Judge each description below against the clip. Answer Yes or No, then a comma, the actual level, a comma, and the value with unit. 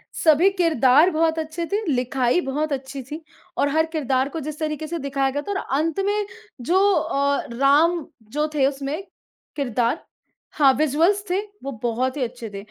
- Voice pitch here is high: Yes, very high, 295 Hz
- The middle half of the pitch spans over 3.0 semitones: Yes, average, 3.5 semitones